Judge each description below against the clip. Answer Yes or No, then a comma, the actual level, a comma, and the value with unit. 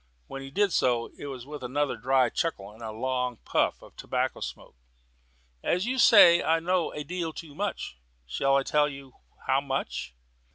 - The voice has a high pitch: No, medium, 140 Hz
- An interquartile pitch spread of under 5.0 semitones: Yes, average, 4.6 semitones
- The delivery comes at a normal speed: Yes, average, 180 wpm